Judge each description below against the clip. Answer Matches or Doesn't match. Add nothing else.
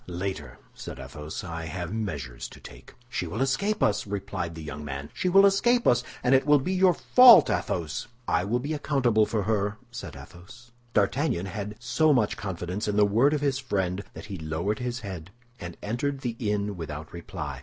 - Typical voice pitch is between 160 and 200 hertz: Doesn't match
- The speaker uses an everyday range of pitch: Doesn't match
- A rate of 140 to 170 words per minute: Doesn't match